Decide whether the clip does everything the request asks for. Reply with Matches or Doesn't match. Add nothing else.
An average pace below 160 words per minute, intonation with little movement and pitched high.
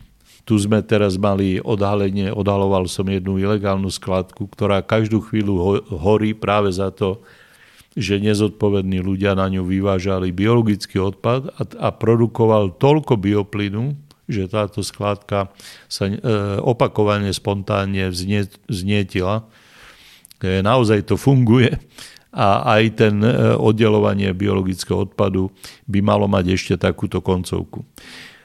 Doesn't match